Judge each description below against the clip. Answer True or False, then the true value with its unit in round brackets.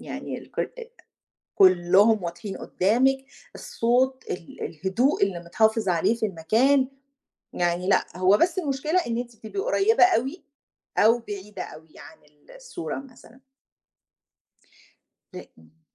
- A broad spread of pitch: True (6.4 semitones)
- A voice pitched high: True (220 Hz)